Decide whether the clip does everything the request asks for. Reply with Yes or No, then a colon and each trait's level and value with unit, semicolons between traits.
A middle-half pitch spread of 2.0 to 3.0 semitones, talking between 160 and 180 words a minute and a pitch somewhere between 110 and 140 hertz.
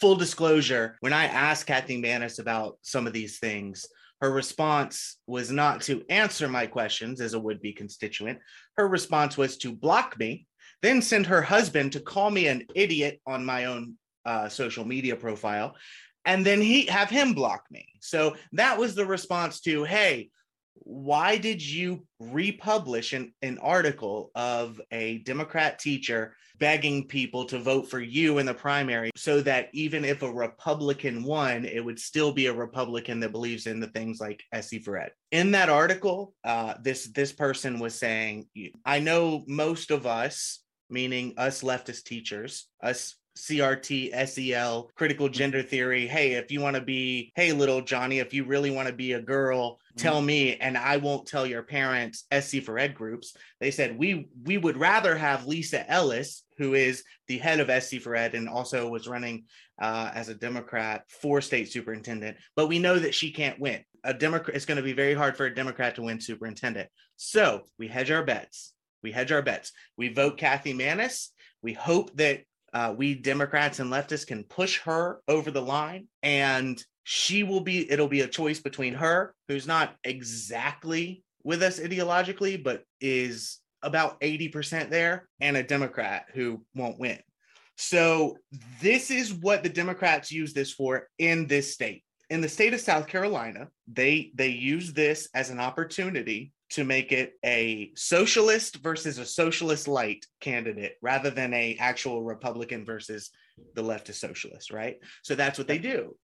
No: average, 4.6 semitones; average, 175 wpm; low, 135 Hz